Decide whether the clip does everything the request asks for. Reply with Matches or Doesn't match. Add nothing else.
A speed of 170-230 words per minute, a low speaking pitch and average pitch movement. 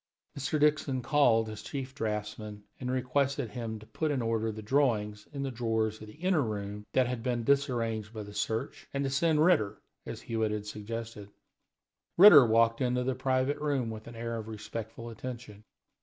Matches